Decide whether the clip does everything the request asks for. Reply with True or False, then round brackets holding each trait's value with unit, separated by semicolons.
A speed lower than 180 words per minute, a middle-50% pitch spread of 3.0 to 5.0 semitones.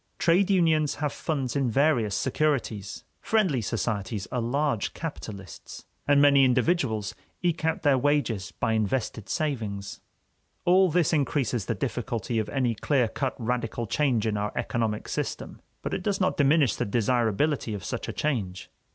False (150 wpm; 5.4 semitones)